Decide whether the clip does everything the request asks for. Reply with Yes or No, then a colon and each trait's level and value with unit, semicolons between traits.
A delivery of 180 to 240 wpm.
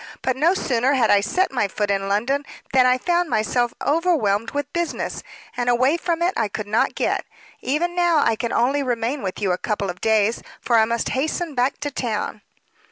Yes: fast, 205 wpm